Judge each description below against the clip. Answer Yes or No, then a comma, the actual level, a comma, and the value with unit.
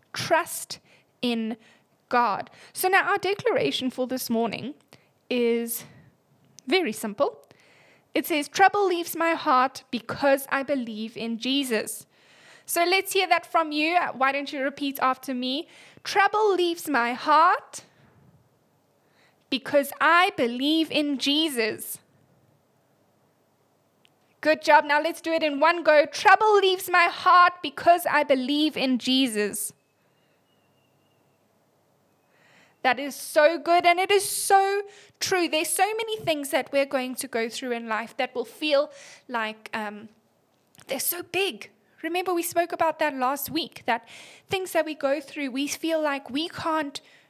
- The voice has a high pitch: Yes, very high, 295 Hz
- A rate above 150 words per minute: No, average, 140 wpm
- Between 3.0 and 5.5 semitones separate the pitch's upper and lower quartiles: Yes, average, 5.0 semitones